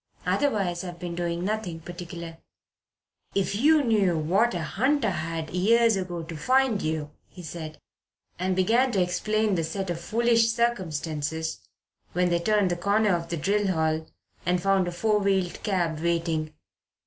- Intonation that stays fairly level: No, average, 4.1 semitones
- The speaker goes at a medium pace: Yes, average, 160 wpm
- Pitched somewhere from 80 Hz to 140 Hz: No, medium, 180 Hz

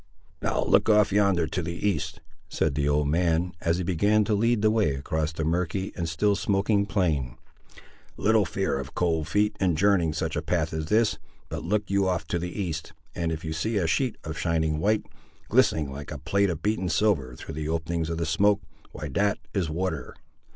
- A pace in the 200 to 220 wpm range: Yes, fast, 205 wpm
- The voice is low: Yes, very low, 85 Hz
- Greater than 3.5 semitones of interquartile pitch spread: Yes, average, 4.2 semitones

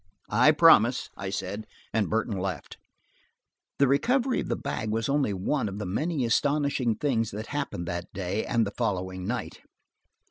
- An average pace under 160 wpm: No, average, 165 wpm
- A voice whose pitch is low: Yes, low, 110 Hz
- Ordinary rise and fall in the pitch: No, wide, 6.2 semitones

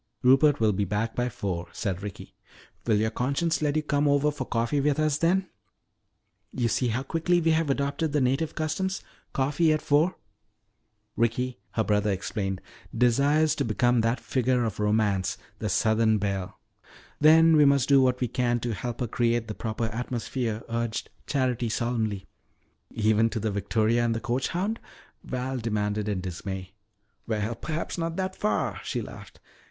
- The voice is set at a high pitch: No, low, 120 Hz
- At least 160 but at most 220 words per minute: Yes, average, 170 wpm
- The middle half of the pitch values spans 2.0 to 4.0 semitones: No, average, 4.9 semitones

